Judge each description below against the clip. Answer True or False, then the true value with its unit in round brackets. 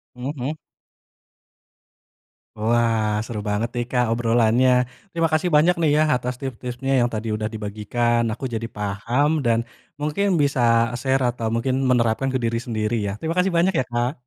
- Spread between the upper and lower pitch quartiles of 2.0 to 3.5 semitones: True (2.9 semitones)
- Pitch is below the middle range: True (120 Hz)